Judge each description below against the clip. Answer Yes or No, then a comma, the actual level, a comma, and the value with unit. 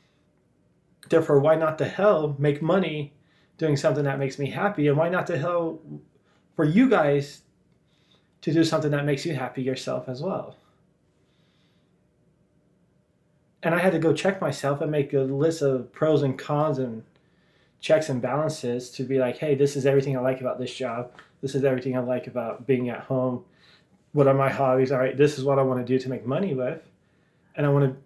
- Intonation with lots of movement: No, average, 3.4 semitones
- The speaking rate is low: No, average, 195 wpm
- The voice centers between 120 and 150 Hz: Yes, medium, 140 Hz